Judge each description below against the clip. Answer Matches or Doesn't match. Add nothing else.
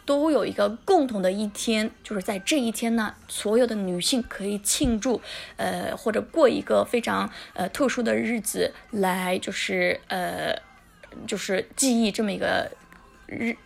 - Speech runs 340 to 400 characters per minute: Doesn't match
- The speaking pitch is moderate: Doesn't match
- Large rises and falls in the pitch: Doesn't match